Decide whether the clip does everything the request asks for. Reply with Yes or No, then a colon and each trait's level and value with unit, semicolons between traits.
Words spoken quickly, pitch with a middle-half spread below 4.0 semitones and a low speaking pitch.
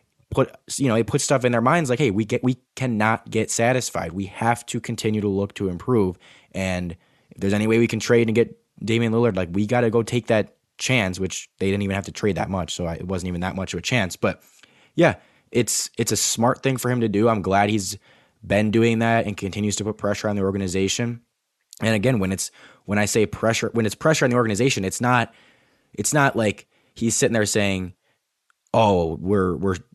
Yes: fast, 230 wpm; average, 3.4 semitones; low, 110 Hz